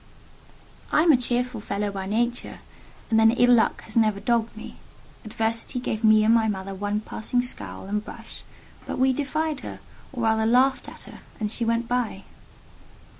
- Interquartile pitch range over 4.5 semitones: No, narrow, 2.5 semitones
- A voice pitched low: No, high, 225 Hz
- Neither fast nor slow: Yes, average, 175 wpm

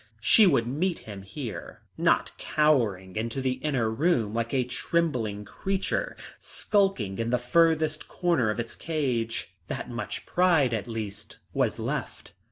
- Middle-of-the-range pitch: No, low, 125 Hz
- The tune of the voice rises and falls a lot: Yes, wide, 6.0 semitones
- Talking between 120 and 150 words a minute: Yes, average, 145 wpm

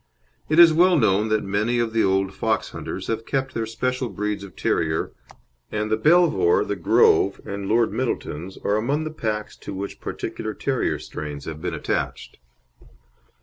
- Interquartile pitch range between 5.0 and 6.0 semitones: Yes, average, 5.3 semitones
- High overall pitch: No, low, 110 Hz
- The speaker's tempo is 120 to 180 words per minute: Yes, average, 170 wpm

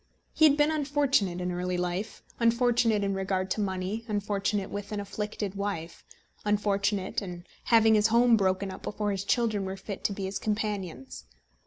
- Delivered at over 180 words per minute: No, average, 170 wpm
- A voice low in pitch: No, high, 205 Hz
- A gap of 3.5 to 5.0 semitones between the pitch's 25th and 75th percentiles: No, narrow, 2.5 semitones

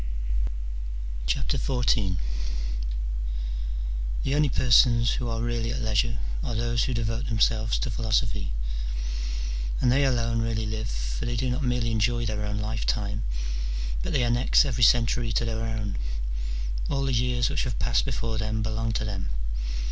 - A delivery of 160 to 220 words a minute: No, average, 150 wpm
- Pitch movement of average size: No, narrow, 2.0 semitones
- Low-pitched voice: Yes, low, 115 Hz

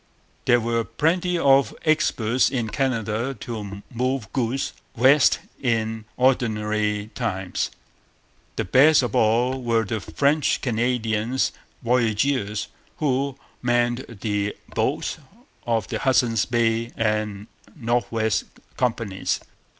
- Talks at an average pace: No, slow, 105 wpm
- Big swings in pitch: No, average, 3.1 semitones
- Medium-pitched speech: No, low, 115 Hz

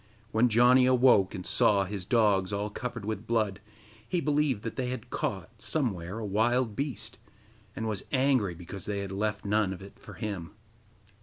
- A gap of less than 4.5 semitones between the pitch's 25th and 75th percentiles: Yes, average, 3.9 semitones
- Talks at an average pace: Yes, average, 175 wpm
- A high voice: No, low, 110 Hz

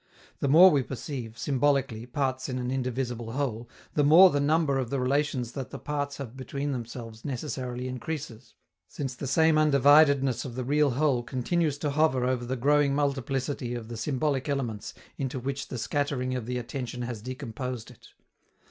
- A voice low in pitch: Yes, low, 130 Hz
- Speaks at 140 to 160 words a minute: No, average, 175 wpm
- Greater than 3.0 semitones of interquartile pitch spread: No, narrow, 2.6 semitones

